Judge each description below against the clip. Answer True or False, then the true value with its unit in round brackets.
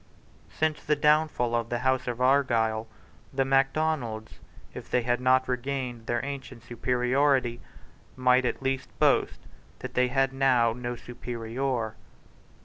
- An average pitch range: False (2.1 semitones)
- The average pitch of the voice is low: True (125 Hz)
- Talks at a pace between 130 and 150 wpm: True (135 wpm)